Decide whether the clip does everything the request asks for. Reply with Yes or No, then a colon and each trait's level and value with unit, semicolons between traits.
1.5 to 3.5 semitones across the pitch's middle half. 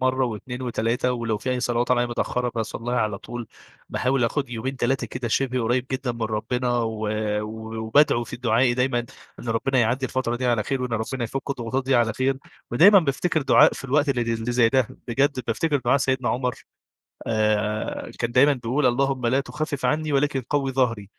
Yes: narrow, 2.4 semitones